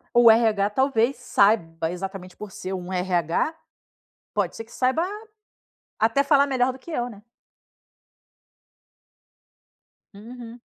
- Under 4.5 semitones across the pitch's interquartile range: No, average, 4.8 semitones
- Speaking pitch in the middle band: No, high, 225 Hz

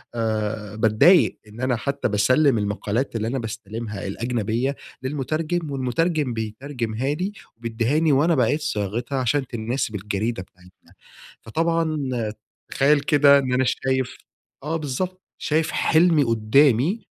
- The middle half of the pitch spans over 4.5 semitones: Yes, average, 5.1 semitones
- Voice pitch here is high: No, low, 130 Hz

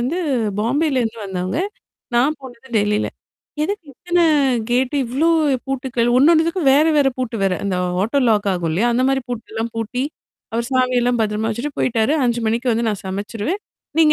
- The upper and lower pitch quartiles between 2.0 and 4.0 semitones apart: Yes, average, 3.6 semitones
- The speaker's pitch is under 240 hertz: No, high, 245 Hz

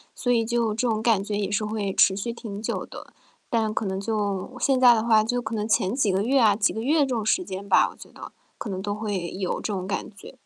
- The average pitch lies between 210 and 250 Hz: Yes, high, 215 Hz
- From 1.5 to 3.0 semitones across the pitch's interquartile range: Yes, average, 2.7 semitones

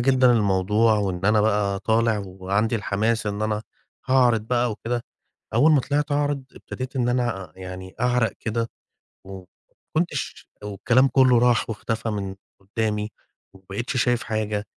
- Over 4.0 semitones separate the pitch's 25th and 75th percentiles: No, average, 3.3 semitones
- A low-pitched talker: Yes, low, 110 Hz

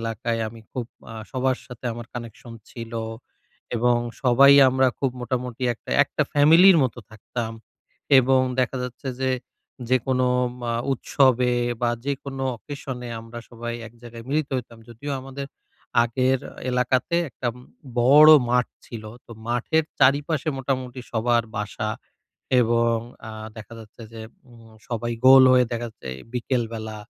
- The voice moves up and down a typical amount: No, narrow, 2.2 semitones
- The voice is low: Yes, low, 125 Hz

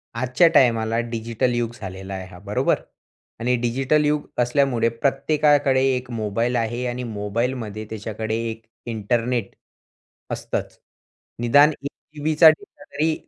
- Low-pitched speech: Yes, low, 120 Hz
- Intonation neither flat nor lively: Yes, average, 3.5 semitones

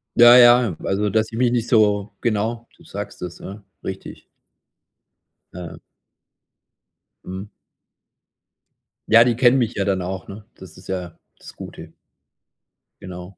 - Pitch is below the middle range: Yes, low, 105 Hz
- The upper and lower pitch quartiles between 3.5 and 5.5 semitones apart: Yes, average, 3.8 semitones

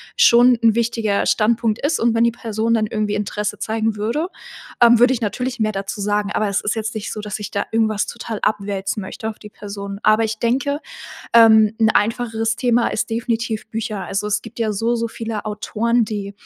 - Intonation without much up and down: Yes, narrow, 1.8 semitones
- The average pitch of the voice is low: No, high, 220 Hz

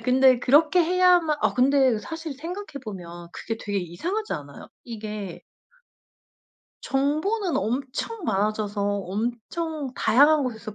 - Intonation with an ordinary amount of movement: No, wide, 7.1 semitones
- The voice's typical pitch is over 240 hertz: Yes, very high, 260 Hz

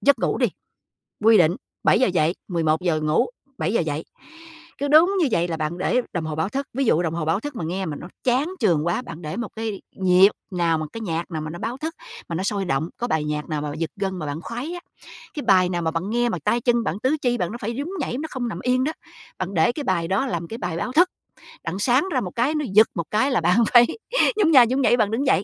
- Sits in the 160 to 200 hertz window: Yes, high, 195 Hz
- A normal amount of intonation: No, wide, 6.9 semitones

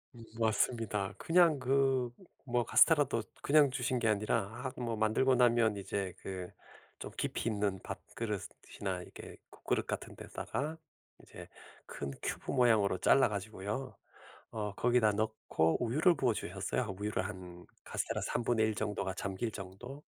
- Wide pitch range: No, average, 3.9 semitones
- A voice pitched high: No, low, 110 Hz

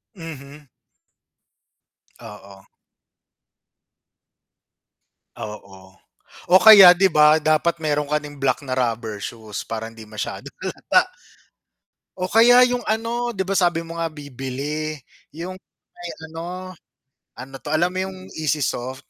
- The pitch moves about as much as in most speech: No, wide, 5.8 semitones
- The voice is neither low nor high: Yes, medium, 150 Hz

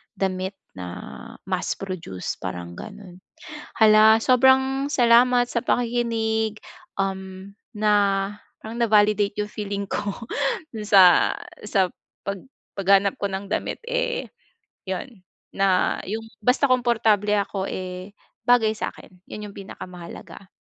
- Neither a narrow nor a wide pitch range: Yes, average, 3.2 semitones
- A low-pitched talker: No, high, 205 Hz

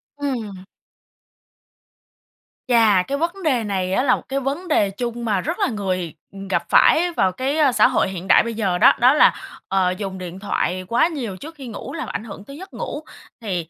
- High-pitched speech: Yes, high, 230 Hz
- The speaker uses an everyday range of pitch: No, wide, 6.8 semitones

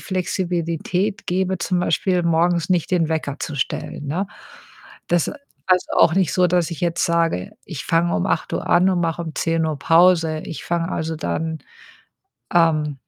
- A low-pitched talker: No, medium, 170 Hz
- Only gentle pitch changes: Yes, narrow, 1.9 semitones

